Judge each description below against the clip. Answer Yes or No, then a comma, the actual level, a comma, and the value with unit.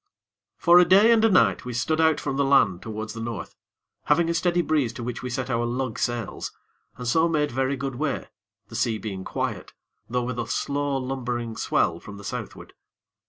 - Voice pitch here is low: Yes, low, 125 Hz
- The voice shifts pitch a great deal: No, average, 4.4 semitones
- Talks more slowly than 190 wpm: No, fast, 205 wpm